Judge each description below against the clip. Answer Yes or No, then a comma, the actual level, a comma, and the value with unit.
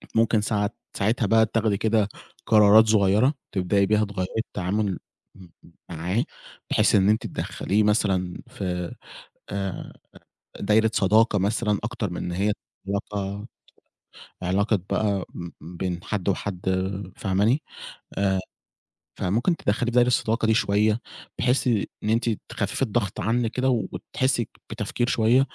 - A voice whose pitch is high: No, low, 105 Hz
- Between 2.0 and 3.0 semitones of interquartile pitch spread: Yes, narrow, 2.5 semitones